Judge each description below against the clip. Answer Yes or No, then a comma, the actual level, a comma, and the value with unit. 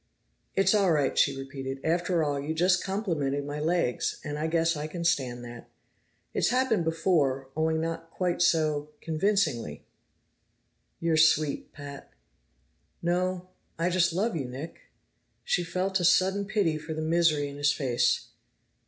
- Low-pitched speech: No, medium, 160 Hz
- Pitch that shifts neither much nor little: Yes, average, 3.7 semitones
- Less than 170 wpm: Yes, average, 150 wpm